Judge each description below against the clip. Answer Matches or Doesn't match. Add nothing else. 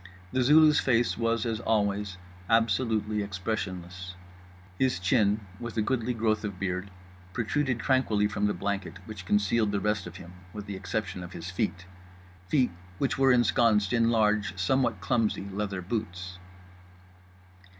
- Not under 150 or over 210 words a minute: Doesn't match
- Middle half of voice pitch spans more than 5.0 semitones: Doesn't match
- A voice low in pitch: Matches